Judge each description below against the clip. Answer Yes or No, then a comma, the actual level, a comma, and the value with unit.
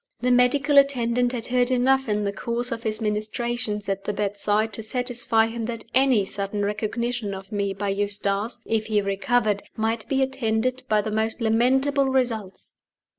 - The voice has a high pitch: Yes, high, 225 Hz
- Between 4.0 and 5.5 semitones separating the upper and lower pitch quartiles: No, average, 3.0 semitones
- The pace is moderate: Yes, average, 170 wpm